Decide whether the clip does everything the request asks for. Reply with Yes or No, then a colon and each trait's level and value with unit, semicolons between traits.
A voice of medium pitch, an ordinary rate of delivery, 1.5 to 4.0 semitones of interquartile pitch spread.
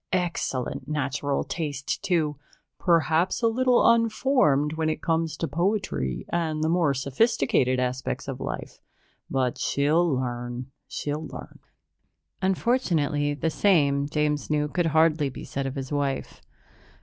No: medium, 150 Hz; slow, 130 wpm; average, 3.7 semitones